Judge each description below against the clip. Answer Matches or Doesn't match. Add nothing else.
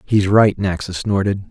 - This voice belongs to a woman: Doesn't match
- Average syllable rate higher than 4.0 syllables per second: Matches